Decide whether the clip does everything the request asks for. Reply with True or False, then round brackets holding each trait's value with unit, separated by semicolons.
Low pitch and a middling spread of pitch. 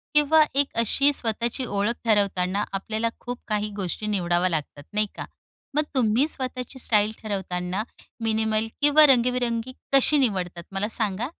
False (220 Hz; 4.1 semitones)